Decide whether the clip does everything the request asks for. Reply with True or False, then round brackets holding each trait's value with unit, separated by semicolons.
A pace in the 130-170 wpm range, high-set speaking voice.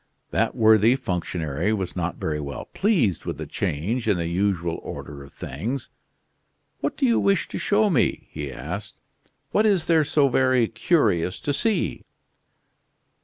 False (155 wpm; 105 Hz)